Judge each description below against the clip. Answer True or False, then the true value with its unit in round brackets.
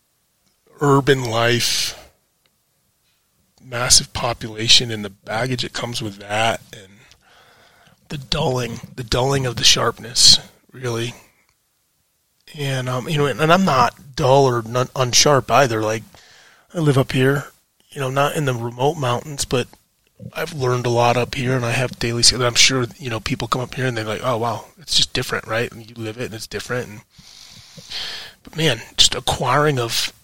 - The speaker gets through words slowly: False (170 wpm)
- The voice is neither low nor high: False (125 Hz)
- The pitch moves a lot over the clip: False (2.9 semitones)